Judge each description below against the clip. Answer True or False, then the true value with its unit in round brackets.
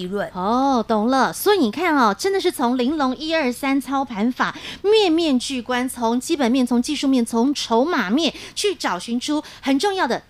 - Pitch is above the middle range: True (260 Hz)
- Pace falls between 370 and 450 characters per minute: False (270 characters per minute)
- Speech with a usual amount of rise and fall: True (4.1 semitones)